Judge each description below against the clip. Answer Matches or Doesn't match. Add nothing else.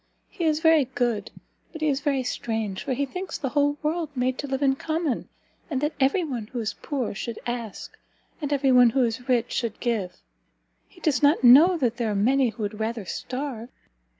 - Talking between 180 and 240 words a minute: Matches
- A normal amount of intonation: Matches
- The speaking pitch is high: Matches